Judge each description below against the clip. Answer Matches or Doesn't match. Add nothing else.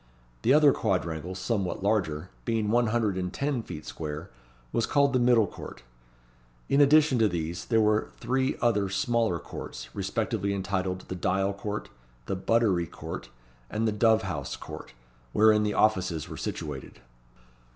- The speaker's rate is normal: Matches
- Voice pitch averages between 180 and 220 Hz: Doesn't match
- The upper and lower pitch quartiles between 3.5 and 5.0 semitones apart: Matches